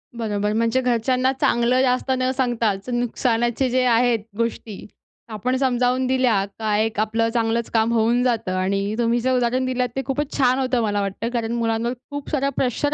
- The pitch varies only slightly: Yes, narrow, 2.2 semitones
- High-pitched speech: Yes, high, 235 Hz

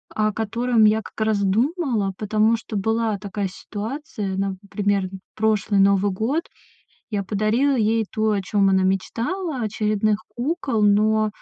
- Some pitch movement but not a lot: No, narrow, 2.2 semitones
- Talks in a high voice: Yes, high, 215 Hz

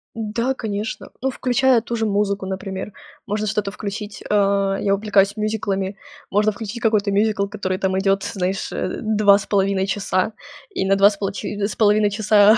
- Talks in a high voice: Yes, high, 205 Hz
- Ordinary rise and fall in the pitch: No, narrow, 1.6 semitones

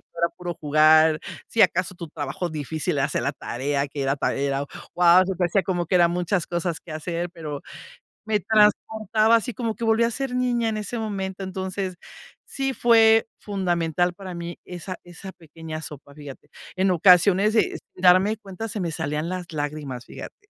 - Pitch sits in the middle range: Yes, medium, 180 Hz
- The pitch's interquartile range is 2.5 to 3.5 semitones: No, average, 4.8 semitones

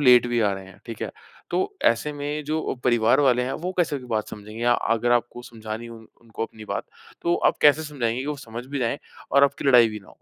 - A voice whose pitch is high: No, low, 120 Hz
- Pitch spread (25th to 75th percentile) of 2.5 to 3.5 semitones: No, average, 4.0 semitones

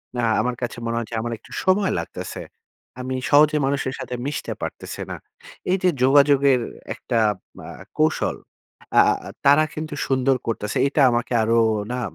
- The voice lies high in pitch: No, low, 135 Hz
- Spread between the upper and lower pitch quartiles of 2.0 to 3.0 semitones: No, average, 3.5 semitones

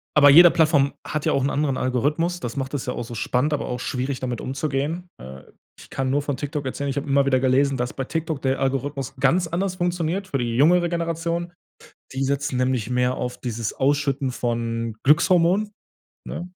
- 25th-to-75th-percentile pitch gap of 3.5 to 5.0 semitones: Yes, average, 4.0 semitones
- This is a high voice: No, medium, 140 Hz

